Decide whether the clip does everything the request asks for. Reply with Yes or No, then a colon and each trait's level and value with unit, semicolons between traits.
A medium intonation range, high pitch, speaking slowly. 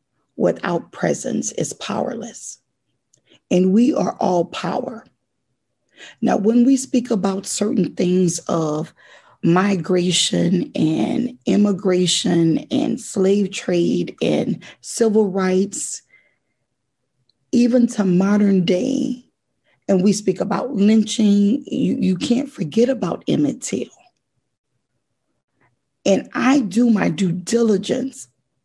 Yes: average, 5.0 semitones; high, 200 Hz; slow, 100 wpm